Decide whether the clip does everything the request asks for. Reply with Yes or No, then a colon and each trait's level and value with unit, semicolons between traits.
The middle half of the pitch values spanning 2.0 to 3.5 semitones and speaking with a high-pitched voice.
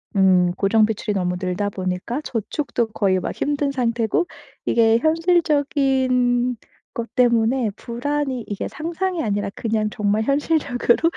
No: average, 5.1 semitones; high, 235 Hz